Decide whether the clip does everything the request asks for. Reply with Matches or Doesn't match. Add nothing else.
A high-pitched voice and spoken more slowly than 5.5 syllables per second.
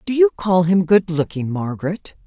Doesn't match